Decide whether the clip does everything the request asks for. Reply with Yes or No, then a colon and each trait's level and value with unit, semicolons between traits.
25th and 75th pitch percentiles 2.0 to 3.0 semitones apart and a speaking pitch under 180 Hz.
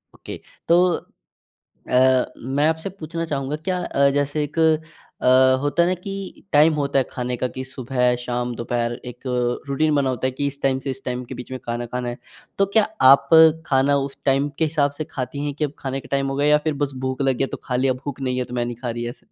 Yes: narrow, 2.6 semitones; low, 135 Hz